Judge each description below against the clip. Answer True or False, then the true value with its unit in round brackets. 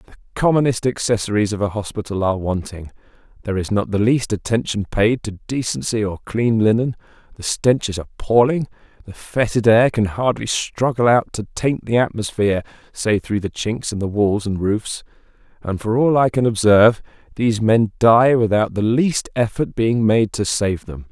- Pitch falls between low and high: False (110 Hz)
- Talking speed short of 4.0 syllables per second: False (5.0 syllables/s)